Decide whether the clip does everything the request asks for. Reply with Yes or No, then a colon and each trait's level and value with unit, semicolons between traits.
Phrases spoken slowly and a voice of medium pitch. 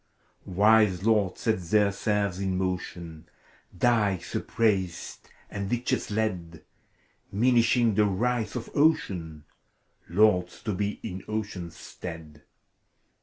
No: slow, 105 wpm; low, 100 Hz